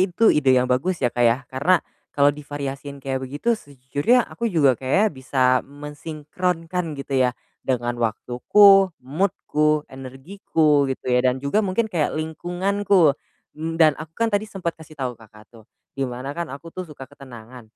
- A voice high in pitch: No, medium, 145 Hz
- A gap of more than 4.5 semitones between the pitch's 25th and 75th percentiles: Yes, average, 5.2 semitones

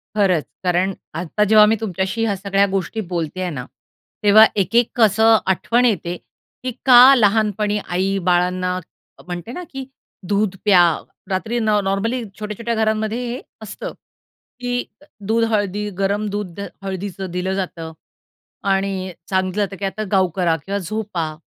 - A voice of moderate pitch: No, high, 200 Hz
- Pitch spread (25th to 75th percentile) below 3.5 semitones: Yes, average, 2.8 semitones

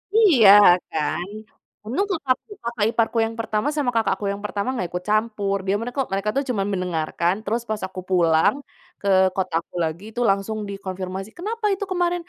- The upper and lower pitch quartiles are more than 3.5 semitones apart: Yes, average, 4.7 semitones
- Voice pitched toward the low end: No, high, 210 Hz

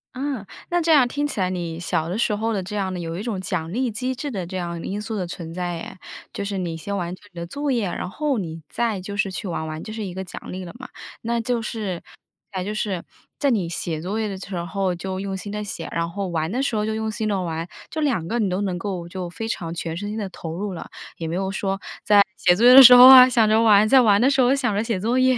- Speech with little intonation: No, average, 4.3 semitones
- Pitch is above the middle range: Yes, high, 200 Hz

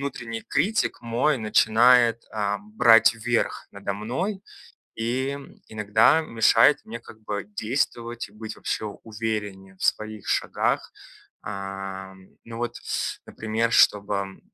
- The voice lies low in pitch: Yes, low, 115 Hz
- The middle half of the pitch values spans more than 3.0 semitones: No, narrow, 2.4 semitones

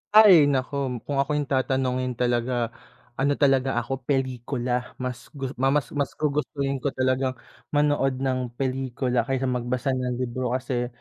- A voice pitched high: No, low, 130 Hz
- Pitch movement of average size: No, narrow, 1.4 semitones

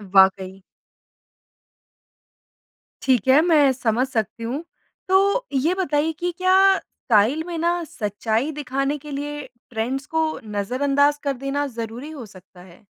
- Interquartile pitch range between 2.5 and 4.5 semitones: No, average, 5.2 semitones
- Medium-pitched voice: No, very high, 275 Hz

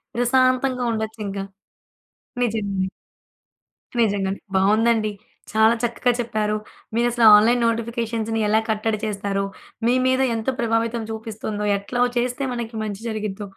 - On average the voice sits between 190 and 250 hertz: Yes, high, 225 Hz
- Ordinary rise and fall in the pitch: No, narrow, 2.1 semitones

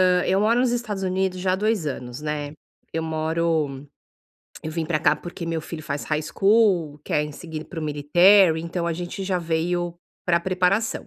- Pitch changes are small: No, average, 3.3 semitones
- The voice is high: No, medium, 170 Hz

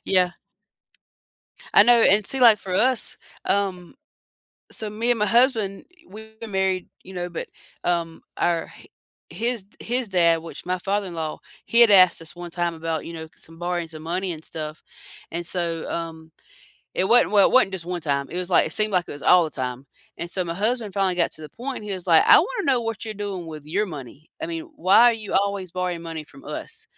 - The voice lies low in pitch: No, medium, 185 Hz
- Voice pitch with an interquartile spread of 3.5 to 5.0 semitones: Yes, average, 4.2 semitones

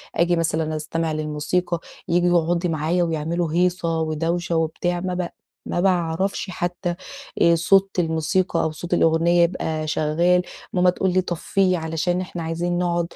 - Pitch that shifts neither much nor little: No, narrow, 1.6 semitones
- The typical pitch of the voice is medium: Yes, medium, 170 Hz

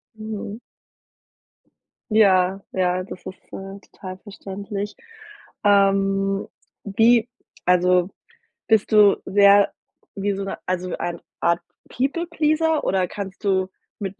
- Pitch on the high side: Yes, high, 195 Hz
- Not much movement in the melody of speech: Yes, narrow, 1.9 semitones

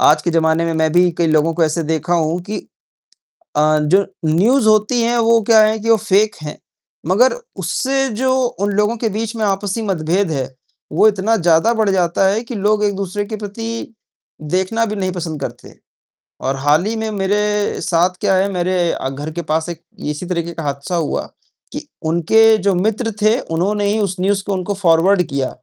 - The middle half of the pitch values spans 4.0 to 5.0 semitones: Yes, average, 4.5 semitones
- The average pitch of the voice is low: No, high, 190 Hz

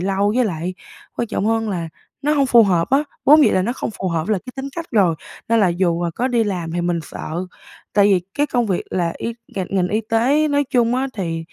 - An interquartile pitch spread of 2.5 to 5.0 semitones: No, wide, 5.5 semitones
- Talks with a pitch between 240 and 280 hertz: No, high, 205 Hz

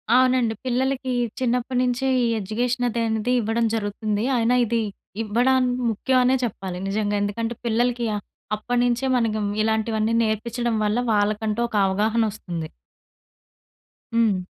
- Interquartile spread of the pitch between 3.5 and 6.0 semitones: No, narrow, 2.5 semitones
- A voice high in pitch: Yes, high, 230 Hz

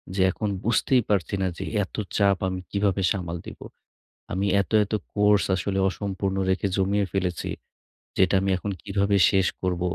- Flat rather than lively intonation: Yes, narrow, 1.4 semitones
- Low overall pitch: Yes, very low, 95 Hz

